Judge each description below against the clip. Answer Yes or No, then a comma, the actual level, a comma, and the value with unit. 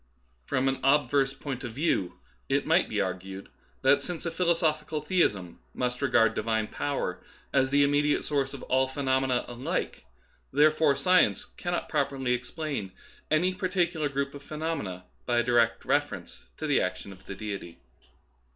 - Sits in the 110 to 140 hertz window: Yes, low, 135 Hz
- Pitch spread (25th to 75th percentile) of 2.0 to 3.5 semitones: No, average, 4.4 semitones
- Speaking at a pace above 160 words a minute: No, average, 155 wpm